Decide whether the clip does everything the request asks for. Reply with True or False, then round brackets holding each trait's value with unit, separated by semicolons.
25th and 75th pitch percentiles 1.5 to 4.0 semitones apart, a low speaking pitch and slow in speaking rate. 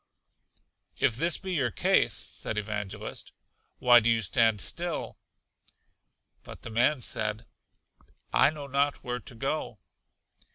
False (4.7 semitones; 120 Hz; 125 wpm)